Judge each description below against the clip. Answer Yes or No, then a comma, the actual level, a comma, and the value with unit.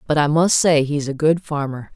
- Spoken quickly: Yes, fast, 245 wpm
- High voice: No, medium, 150 Hz